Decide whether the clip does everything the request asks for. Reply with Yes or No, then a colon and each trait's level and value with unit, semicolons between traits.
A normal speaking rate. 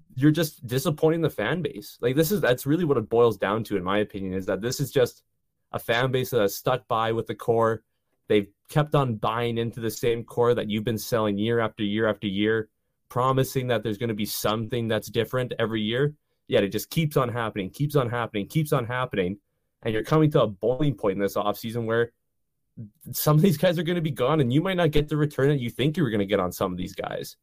No: fast, 250 wpm